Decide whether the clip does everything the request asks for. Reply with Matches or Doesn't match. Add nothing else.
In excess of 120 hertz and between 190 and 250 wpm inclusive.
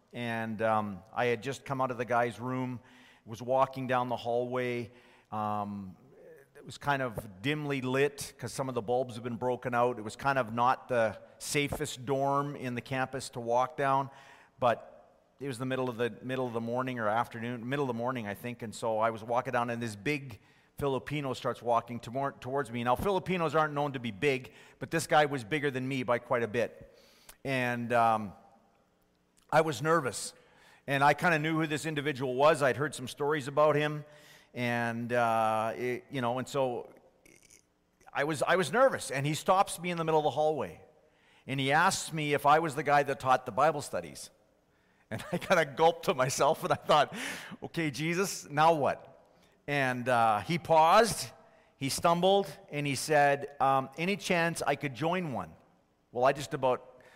Matches